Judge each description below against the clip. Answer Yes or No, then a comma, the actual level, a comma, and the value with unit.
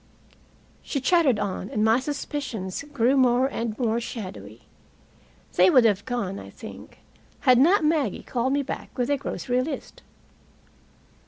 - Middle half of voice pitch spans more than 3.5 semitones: Yes, average, 4.5 semitones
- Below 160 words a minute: Yes, average, 145 wpm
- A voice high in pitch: Yes, high, 245 Hz